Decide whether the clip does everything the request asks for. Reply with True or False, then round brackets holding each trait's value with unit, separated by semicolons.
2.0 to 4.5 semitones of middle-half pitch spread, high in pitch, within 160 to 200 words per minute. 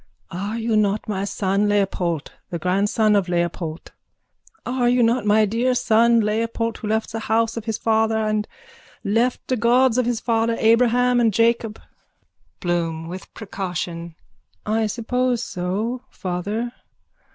False (2.9 semitones; 220 Hz; 145 wpm)